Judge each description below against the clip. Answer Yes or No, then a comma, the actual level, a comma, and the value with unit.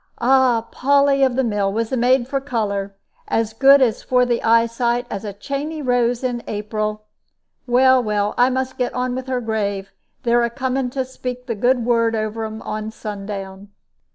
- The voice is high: Yes, high, 240 Hz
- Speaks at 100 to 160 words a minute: No, average, 180 wpm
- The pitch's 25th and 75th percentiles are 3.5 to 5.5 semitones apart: No, average, 3.1 semitones